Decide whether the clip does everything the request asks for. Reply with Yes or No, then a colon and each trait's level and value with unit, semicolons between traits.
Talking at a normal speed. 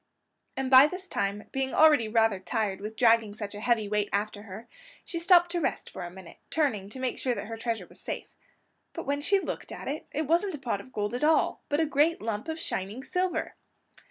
No: fast, 225 wpm